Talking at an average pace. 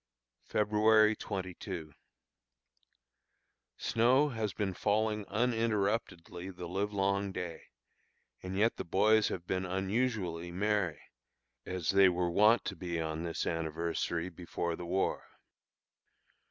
No: slow, 110 wpm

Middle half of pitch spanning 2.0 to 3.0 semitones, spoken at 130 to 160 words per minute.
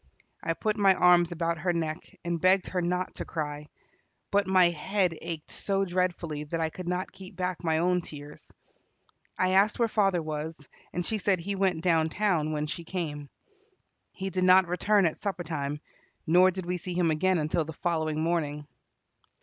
No: average, 2.7 semitones; average, 185 wpm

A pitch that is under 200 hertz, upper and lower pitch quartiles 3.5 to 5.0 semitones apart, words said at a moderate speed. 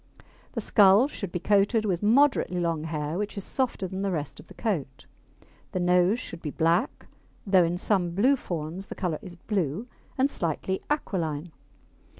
Yes: medium, 185 Hz; average, 3.8 semitones; average, 170 wpm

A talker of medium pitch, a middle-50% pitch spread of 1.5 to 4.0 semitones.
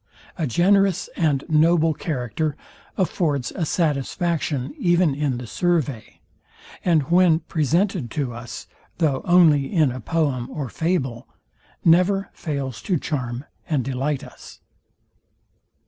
No: medium, 155 Hz; average, 4.5 semitones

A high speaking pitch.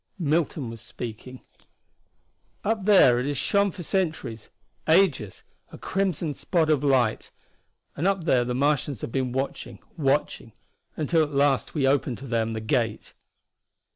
No: medium, 140 Hz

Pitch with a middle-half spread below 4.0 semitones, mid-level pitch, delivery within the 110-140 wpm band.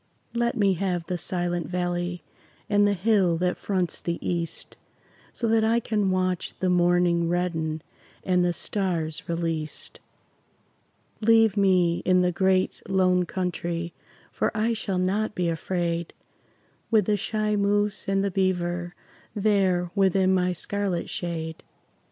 Yes: narrow, 2.5 semitones; medium, 180 Hz; slow, 135 wpm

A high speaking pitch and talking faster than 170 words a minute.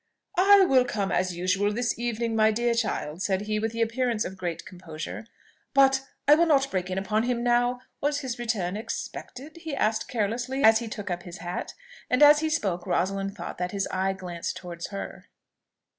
Yes: high, 220 Hz; average, 195 wpm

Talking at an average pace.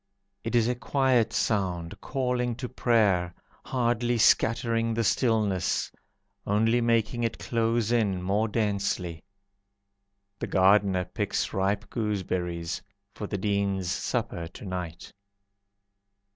No: slow, 110 wpm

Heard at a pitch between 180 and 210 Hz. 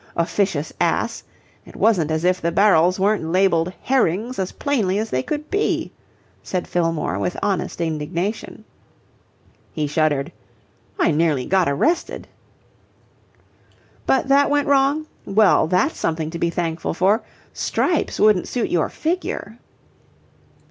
Yes: medium, 185 Hz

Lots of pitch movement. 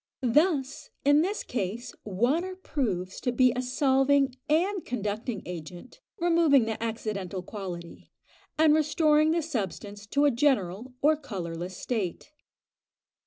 Yes: wide, 7.0 semitones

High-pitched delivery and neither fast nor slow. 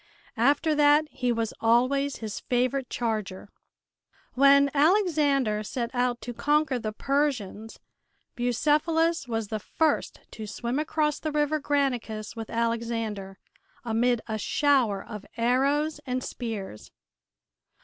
No: very high, 250 Hz; slow, 120 wpm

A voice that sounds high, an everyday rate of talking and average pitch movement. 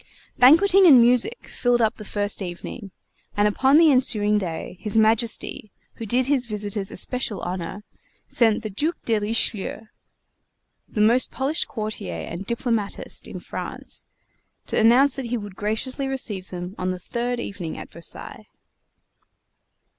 Yes: high, 220 Hz; average, 145 wpm; average, 3.7 semitones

